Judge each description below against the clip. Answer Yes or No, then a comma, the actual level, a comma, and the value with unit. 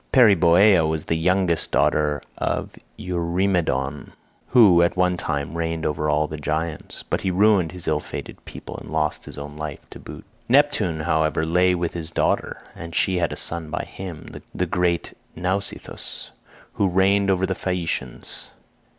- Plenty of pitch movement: No, average, 2.9 semitones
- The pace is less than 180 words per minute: Yes, average, 160 wpm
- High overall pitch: No, very low, 85 Hz